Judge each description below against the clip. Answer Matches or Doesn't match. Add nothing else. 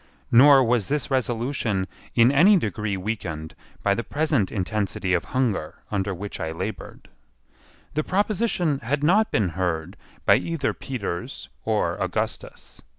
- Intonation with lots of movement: Matches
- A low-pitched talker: Matches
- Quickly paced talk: Doesn't match